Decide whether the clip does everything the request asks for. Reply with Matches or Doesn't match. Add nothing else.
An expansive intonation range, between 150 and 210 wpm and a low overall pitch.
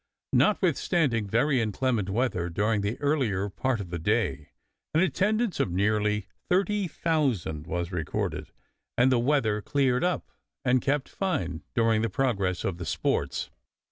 Doesn't match